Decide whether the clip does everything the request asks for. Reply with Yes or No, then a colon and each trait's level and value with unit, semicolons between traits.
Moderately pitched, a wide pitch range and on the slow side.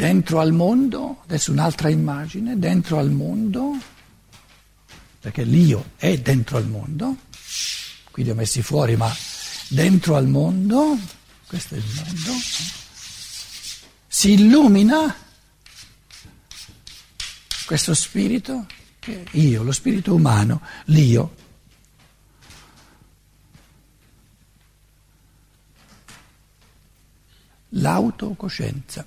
Yes: medium, 160 Hz; wide, 7.7 semitones; slow, 80 wpm